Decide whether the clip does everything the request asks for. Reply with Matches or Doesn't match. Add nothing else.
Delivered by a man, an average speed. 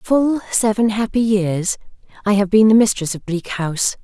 Doesn't match